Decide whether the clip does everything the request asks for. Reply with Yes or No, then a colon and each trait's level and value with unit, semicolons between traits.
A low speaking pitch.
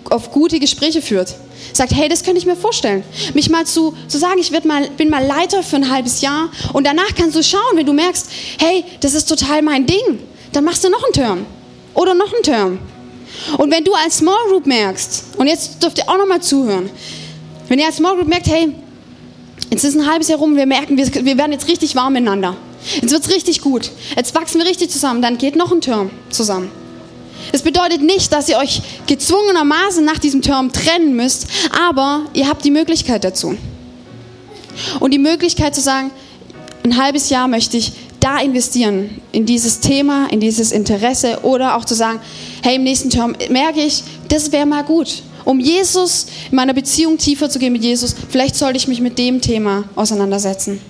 No: very high, 290 Hz